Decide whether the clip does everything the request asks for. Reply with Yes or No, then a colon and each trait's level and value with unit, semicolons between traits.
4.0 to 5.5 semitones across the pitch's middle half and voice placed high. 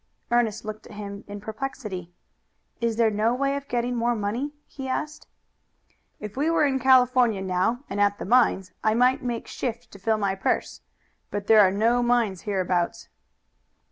No: average, 3.5 semitones; high, 225 Hz